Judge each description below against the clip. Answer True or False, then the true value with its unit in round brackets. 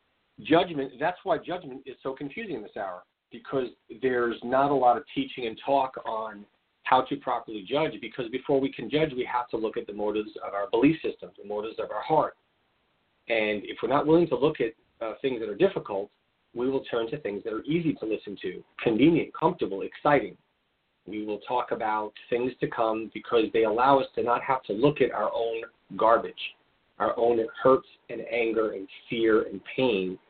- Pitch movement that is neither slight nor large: True (4.0 semitones)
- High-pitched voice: False (120 Hz)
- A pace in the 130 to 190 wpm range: False (200 wpm)